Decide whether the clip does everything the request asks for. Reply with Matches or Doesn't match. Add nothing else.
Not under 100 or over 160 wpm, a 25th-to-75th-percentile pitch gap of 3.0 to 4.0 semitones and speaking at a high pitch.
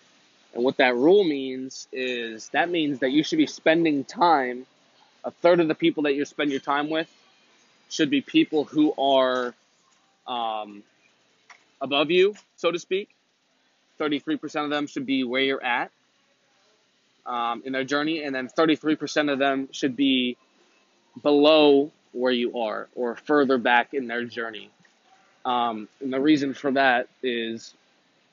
Doesn't match